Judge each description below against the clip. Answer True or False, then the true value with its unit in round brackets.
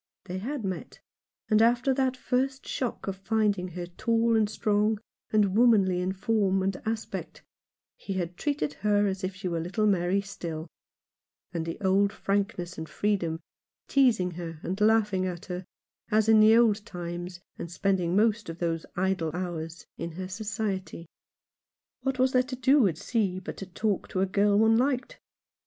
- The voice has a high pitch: True (195 Hz)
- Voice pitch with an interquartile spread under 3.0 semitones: False (3.7 semitones)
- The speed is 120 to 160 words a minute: False (175 wpm)